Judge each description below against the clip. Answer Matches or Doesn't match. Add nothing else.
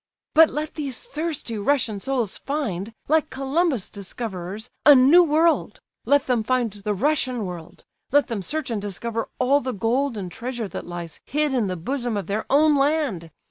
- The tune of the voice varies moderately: Doesn't match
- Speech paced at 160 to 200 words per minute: Matches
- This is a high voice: Matches